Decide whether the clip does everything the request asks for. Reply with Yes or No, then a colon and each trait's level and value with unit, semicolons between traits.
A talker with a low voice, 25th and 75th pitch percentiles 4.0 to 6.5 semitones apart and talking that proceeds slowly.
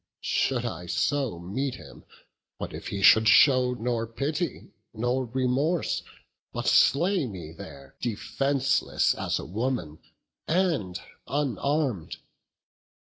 Yes: low, 125 Hz; wide, 5.4 semitones; slow, 110 wpm